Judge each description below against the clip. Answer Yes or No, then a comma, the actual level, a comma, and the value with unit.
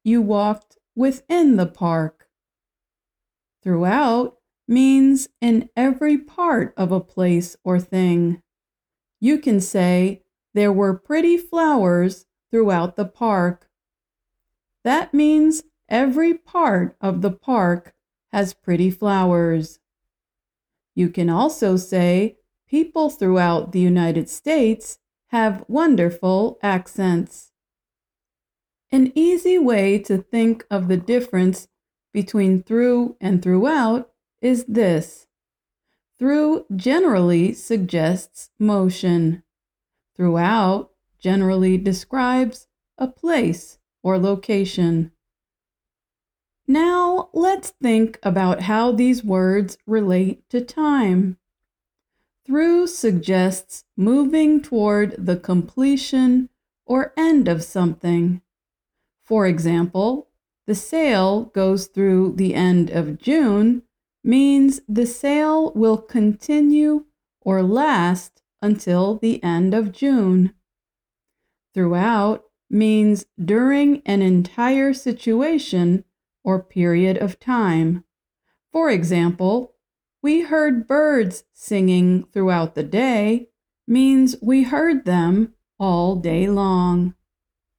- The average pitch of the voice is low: No, high, 205 Hz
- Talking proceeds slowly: Yes, slow, 95 wpm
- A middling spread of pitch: No, wide, 5.9 semitones